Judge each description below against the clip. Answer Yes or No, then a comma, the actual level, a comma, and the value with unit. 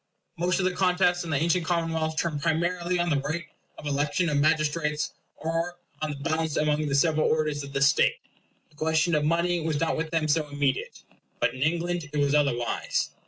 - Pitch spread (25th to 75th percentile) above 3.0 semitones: No, narrow, 2.4 semitones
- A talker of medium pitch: Yes, medium, 155 Hz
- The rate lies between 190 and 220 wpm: Yes, average, 200 wpm